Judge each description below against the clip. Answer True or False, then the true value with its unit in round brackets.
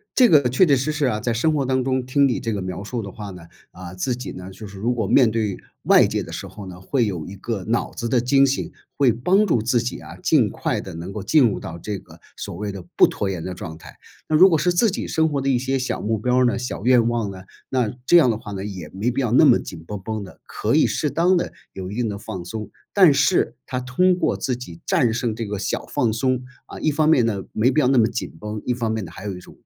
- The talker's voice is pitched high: False (115 Hz)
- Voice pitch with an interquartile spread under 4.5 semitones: False (4.8 semitones)